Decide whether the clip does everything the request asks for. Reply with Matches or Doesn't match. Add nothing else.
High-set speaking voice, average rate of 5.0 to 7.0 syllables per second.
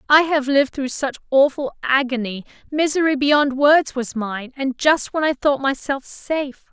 Doesn't match